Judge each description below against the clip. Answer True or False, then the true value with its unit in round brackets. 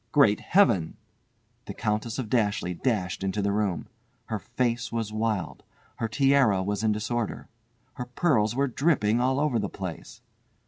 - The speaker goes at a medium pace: True (150 wpm)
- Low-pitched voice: True (110 Hz)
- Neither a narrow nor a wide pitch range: True (3.4 semitones)